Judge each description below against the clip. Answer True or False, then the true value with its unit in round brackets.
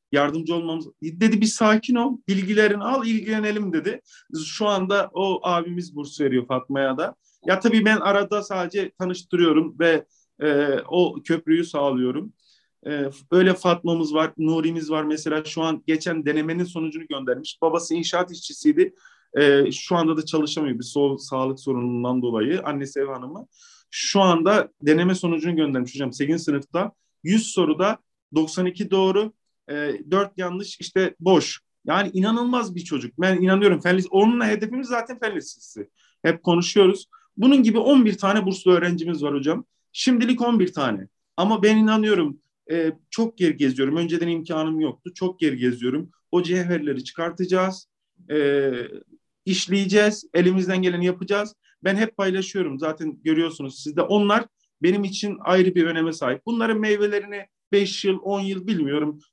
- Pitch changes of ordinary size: True (4.6 semitones)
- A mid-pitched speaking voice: True (175 Hz)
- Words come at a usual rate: False (145 wpm)